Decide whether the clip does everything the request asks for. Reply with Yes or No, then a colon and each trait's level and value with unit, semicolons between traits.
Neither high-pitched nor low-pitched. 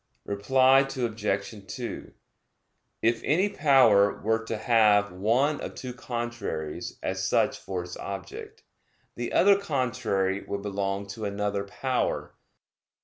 No: low, 115 Hz